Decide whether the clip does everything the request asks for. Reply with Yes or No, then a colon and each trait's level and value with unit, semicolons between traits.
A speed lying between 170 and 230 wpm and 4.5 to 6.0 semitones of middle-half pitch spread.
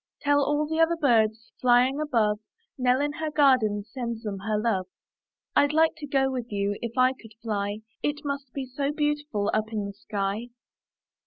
Yes: average, 180 wpm; average, 5.2 semitones